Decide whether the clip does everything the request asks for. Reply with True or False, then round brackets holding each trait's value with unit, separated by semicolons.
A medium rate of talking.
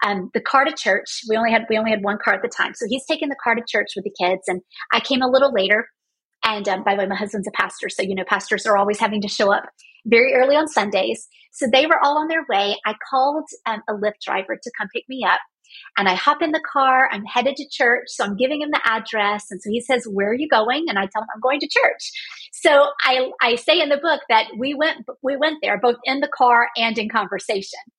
False (270 wpm)